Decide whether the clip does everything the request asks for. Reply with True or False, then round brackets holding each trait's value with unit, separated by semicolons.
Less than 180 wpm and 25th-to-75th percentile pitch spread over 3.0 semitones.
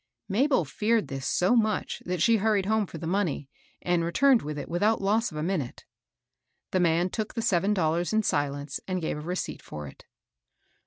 False (195 wpm; 5.2 semitones)